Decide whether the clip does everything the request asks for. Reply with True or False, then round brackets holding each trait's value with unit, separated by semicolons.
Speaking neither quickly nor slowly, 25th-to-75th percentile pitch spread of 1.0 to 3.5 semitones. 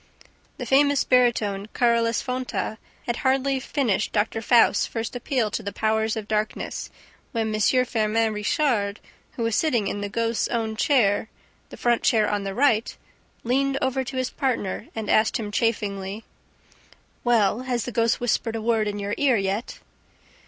True (160 wpm; 2.9 semitones)